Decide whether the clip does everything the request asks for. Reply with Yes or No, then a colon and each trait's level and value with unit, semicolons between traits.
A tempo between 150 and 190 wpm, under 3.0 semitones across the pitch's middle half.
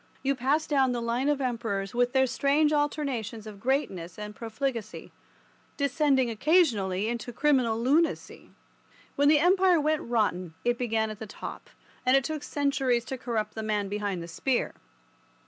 No: average, 165 wpm; average, 4.5 semitones